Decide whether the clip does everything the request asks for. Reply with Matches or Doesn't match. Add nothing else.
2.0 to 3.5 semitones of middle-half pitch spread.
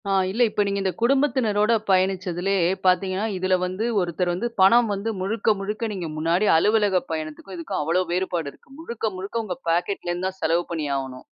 Matches